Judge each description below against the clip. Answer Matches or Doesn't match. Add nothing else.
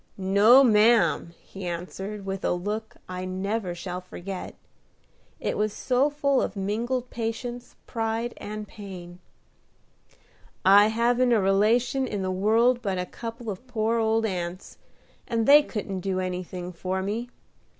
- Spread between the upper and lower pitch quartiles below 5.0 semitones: Matches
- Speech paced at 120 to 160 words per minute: Matches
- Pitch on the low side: Doesn't match